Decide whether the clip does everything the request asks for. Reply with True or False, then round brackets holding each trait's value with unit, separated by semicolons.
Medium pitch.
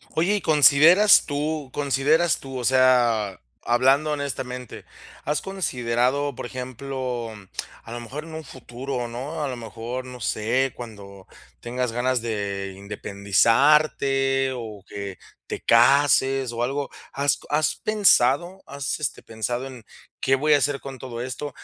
False (130 Hz)